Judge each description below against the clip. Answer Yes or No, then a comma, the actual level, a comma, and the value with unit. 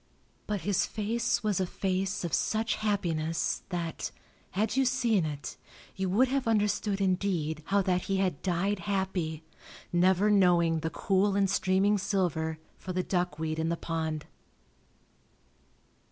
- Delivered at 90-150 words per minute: Yes, average, 140 wpm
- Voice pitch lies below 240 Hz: Yes, high, 190 Hz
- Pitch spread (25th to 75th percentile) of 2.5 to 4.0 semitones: Yes, average, 3.3 semitones